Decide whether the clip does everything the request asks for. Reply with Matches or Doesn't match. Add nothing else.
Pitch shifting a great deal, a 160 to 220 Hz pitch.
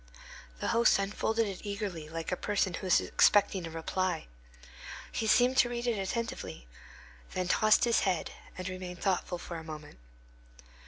Doesn't match